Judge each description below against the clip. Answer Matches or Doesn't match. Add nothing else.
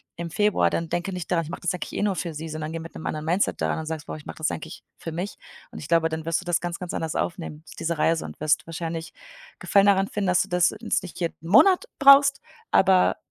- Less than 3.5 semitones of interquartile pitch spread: Matches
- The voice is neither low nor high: Matches